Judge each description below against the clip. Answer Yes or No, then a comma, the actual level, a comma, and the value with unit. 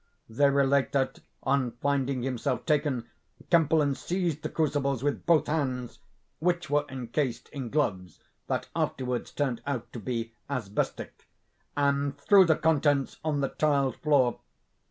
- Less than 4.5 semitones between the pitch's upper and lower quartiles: Yes, average, 2.8 semitones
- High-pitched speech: No, medium, 140 Hz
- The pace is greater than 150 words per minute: No, slow, 135 wpm